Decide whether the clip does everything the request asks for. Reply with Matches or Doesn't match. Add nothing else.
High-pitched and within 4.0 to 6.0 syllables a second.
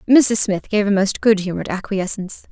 Matches